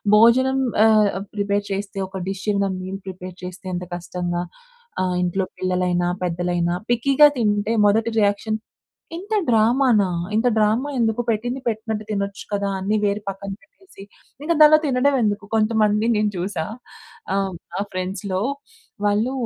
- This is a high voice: Yes, high, 205 Hz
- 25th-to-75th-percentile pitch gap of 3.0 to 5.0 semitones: Yes, average, 3.3 semitones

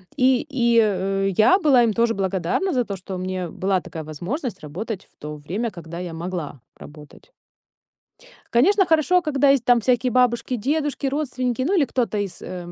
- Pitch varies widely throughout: Yes, wide, 6.4 semitones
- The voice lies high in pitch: Yes, high, 230 Hz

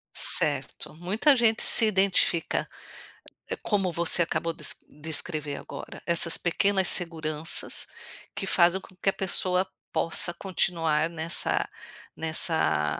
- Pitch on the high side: No, medium, 170 Hz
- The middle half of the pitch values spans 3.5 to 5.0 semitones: No, average, 2.9 semitones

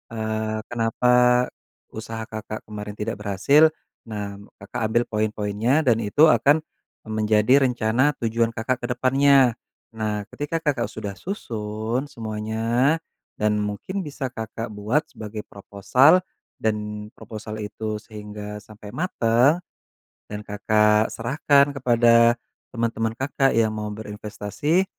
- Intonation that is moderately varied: Yes, average, 3.0 semitones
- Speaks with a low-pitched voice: Yes, low, 110 Hz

